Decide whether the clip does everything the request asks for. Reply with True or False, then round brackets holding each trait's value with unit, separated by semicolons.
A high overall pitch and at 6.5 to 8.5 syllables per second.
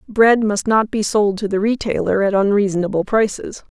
False (205 Hz; 5.1 syllables/s)